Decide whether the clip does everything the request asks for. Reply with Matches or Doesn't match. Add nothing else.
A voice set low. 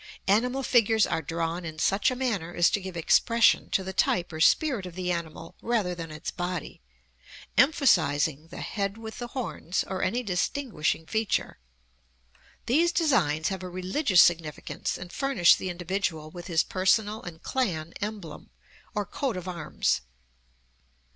Doesn't match